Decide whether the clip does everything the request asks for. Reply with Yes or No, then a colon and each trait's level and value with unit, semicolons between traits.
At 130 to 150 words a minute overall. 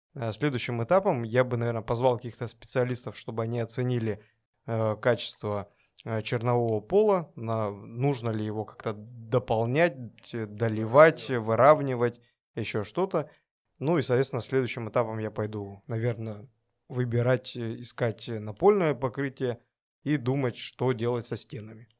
No: average, 115 wpm